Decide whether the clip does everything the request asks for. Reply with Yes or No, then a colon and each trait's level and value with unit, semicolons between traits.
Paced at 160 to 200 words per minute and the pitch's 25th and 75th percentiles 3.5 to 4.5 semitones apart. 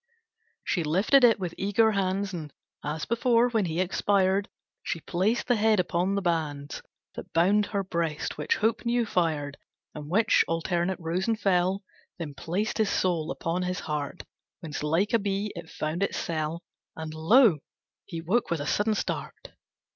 Yes: average, 165 wpm; average, 4.1 semitones